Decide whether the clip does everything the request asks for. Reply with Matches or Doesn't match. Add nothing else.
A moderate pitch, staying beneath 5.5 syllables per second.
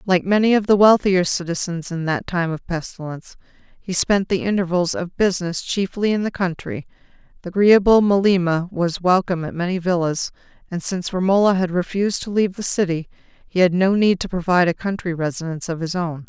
Doesn't match